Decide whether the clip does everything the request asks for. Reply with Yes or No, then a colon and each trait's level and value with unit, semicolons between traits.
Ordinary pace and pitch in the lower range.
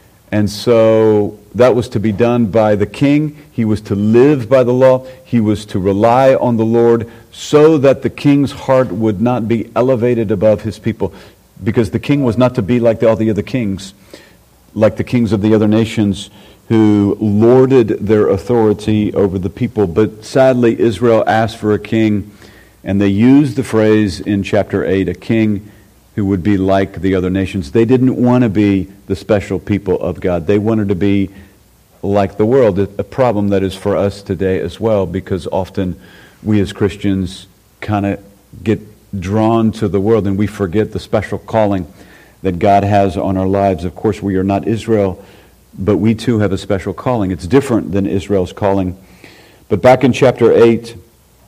Yes: average, 185 wpm; low, 105 Hz